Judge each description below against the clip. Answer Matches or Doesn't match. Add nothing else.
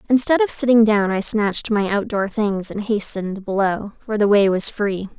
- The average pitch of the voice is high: Matches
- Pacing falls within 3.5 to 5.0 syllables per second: Matches